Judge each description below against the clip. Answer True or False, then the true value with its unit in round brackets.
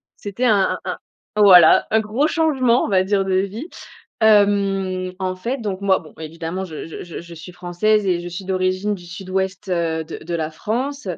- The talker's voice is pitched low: False (190 Hz)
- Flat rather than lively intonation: False (3.1 semitones)